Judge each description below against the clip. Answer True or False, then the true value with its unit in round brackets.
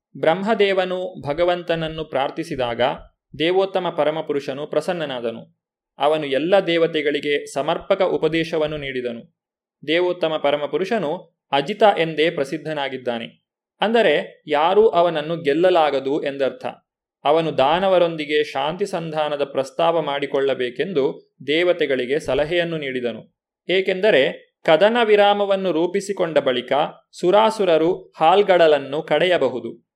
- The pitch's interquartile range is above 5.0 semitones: False (4.3 semitones)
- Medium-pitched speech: True (165 Hz)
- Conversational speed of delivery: True (80 wpm)